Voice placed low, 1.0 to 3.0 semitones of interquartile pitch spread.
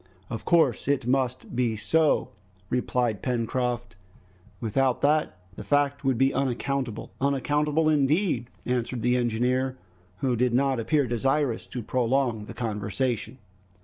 Yes: low, 125 Hz; narrow, 2.6 semitones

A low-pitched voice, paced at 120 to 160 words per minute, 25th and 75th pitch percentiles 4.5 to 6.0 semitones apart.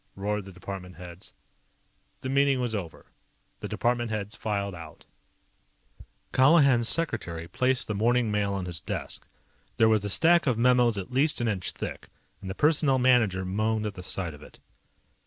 No: low, 110 Hz; average, 175 wpm; average, 4.8 semitones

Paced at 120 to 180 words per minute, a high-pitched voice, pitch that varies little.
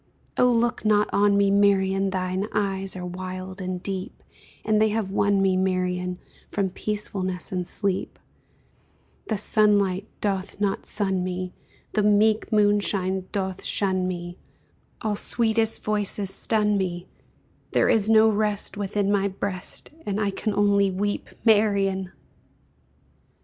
Yes: slow, 135 wpm; high, 200 Hz; narrow, 1.9 semitones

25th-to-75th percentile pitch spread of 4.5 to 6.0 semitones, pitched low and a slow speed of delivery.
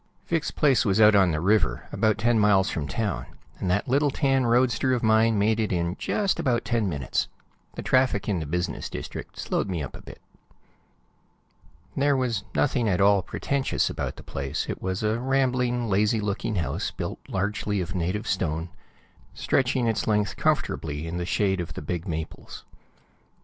No: average, 5.2 semitones; low, 105 Hz; average, 175 wpm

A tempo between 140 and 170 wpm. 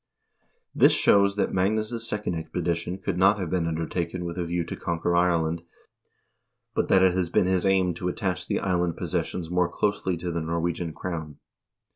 No: average, 180 wpm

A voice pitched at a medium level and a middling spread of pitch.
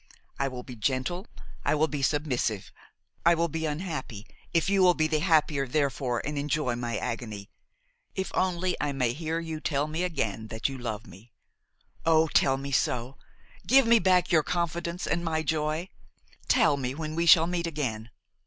Yes: medium, 155 Hz; average, 4.8 semitones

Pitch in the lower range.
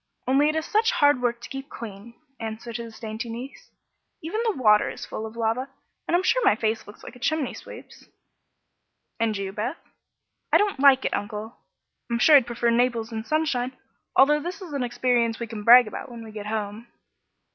No: high, 240 Hz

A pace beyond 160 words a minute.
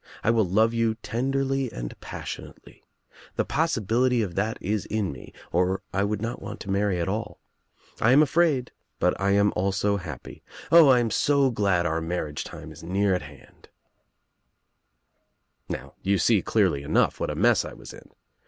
Yes: average, 180 wpm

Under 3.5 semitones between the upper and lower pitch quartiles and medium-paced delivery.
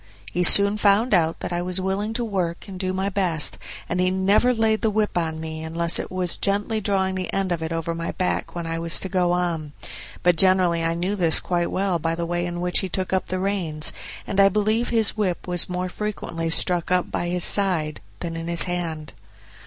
No: average, 2.7 semitones; fast, 225 wpm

